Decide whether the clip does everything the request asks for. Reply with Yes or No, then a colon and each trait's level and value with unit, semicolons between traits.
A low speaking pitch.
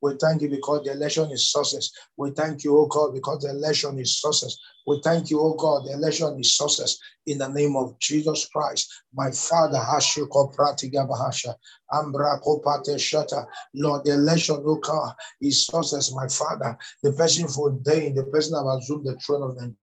No: medium, 145 Hz